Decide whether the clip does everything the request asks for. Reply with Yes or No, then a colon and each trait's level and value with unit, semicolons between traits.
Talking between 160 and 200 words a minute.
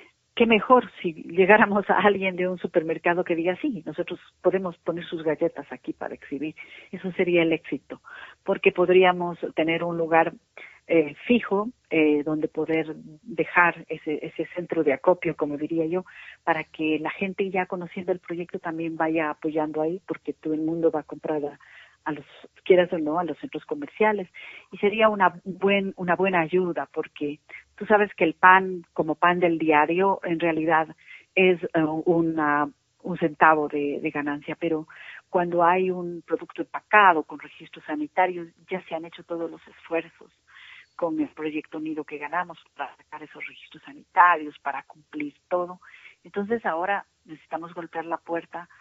Yes: average, 165 wpm